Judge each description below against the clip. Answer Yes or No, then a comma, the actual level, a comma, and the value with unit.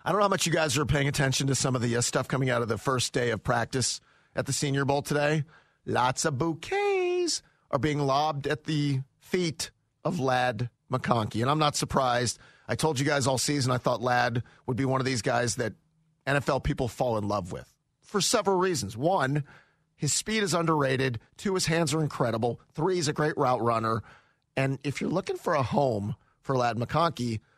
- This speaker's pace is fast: Yes, fast, 210 wpm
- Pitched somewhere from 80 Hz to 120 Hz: No, medium, 140 Hz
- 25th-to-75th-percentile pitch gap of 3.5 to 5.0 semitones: Yes, average, 4.0 semitones